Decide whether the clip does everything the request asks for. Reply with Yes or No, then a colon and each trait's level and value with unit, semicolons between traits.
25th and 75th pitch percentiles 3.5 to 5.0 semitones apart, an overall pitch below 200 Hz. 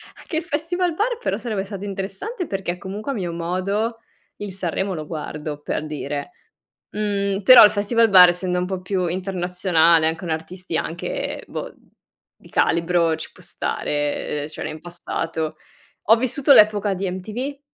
Yes: average, 4.1 semitones; high, 190 Hz